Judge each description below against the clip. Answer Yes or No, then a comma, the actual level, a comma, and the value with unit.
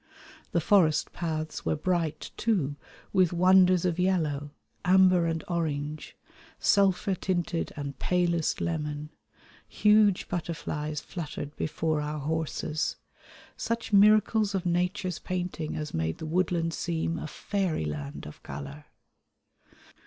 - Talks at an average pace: No, slow, 115 wpm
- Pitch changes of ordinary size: Yes, average, 3.4 semitones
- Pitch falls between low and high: Yes, medium, 165 Hz